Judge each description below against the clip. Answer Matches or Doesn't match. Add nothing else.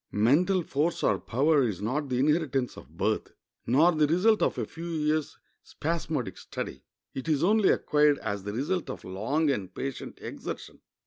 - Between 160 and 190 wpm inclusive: Matches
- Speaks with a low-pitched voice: Doesn't match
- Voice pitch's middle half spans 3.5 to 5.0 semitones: Matches